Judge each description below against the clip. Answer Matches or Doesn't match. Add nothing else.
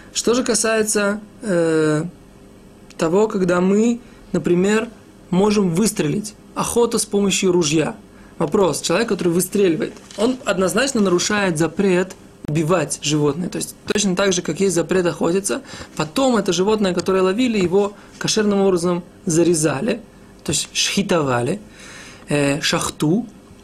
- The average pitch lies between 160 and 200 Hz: Matches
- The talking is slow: Doesn't match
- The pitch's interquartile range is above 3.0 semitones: Matches